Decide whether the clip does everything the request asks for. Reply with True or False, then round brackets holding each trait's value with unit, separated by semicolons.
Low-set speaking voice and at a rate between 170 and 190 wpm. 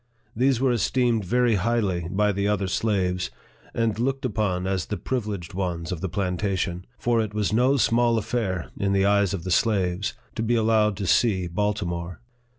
True (100 Hz; 175 wpm)